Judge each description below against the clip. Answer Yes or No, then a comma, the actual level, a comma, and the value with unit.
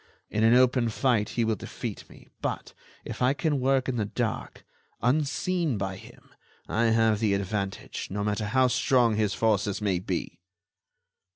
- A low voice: Yes, low, 110 Hz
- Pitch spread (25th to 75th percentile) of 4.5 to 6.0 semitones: No, average, 3.7 semitones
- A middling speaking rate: Yes, average, 165 wpm